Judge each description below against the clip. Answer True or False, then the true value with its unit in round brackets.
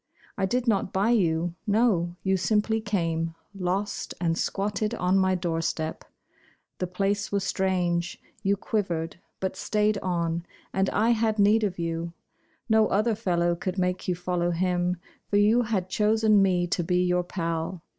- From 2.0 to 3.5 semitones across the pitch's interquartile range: True (3.1 semitones)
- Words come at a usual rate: True (155 wpm)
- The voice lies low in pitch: False (190 Hz)